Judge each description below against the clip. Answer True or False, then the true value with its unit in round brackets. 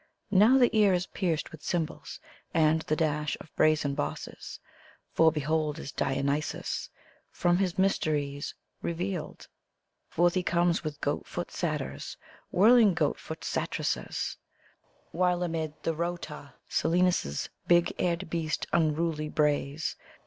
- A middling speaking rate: False (125 wpm)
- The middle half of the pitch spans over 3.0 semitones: False (2.7 semitones)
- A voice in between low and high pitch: True (165 Hz)